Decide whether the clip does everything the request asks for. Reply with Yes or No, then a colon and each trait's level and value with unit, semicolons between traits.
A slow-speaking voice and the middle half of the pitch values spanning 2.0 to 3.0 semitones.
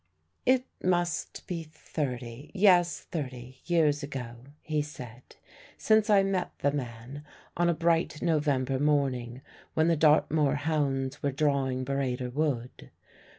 No: slow, 125 wpm; average, 4.0 semitones